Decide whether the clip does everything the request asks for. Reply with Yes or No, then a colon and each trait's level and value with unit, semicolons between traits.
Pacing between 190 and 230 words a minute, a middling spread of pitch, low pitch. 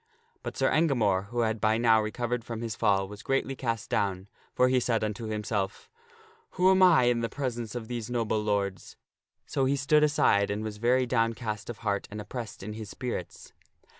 Yes: average, 195 wpm; average, 3.2 semitones; low, 115 Hz